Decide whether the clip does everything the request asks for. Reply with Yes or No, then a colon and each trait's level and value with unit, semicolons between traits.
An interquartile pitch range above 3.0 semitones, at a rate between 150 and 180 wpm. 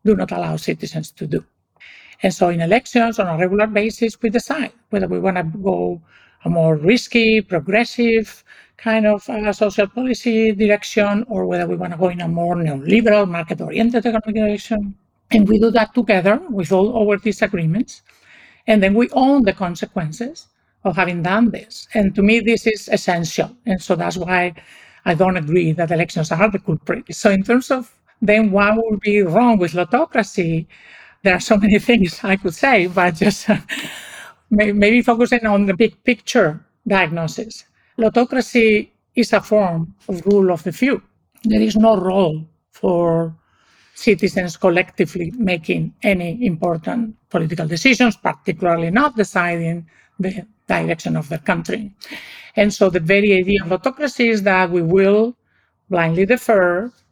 Yes: average, 3.9 semitones; average, 160 wpm